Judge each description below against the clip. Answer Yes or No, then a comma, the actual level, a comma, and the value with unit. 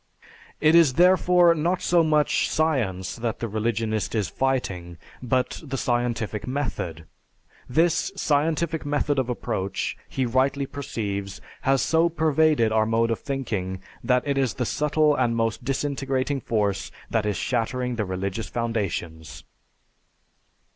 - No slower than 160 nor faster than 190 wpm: No, slow, 135 wpm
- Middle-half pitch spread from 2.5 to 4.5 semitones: No, average, 5.1 semitones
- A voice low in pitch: Yes, low, 125 Hz